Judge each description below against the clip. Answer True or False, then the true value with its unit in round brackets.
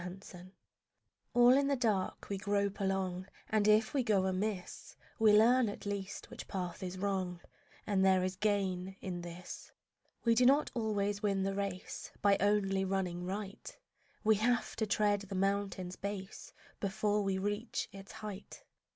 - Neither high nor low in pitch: False (200 Hz)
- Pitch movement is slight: True (1.9 semitones)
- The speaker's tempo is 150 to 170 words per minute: True (160 wpm)